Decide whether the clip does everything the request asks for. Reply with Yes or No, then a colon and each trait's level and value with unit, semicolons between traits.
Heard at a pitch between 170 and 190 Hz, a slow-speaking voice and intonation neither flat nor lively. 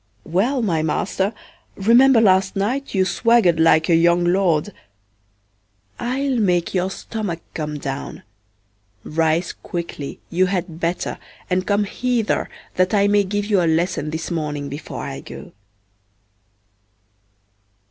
Yes: medium, 185 Hz; slow, 125 wpm; average, 4.0 semitones